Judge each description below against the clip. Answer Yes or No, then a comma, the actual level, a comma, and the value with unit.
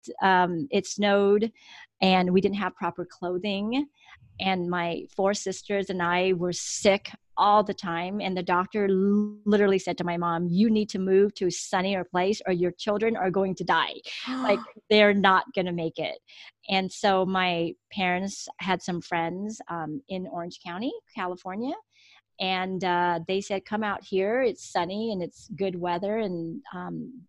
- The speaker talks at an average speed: Yes, average, 170 wpm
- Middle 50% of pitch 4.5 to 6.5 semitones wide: No, narrow, 2.5 semitones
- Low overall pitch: No, high, 190 Hz